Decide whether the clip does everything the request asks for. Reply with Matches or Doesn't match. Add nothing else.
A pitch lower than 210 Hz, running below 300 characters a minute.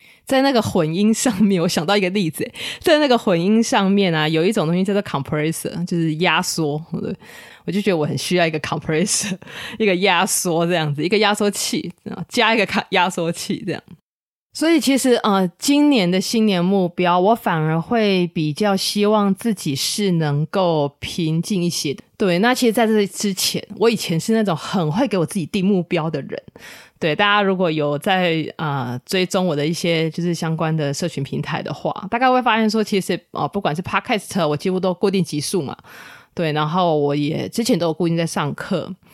Doesn't match